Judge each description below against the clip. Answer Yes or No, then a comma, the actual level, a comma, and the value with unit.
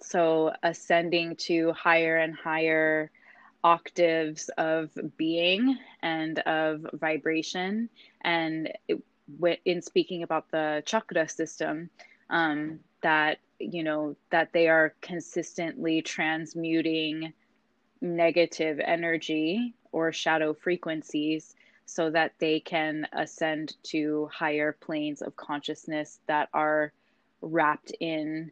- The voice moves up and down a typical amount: No, narrow, 1.5 semitones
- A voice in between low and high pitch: Yes, medium, 160 Hz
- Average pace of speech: No, slow, 100 wpm